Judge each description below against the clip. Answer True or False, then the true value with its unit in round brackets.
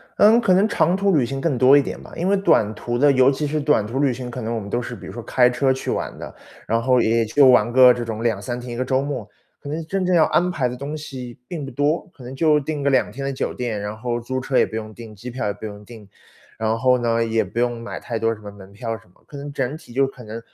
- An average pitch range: True (3.7 semitones)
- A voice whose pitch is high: False (125 Hz)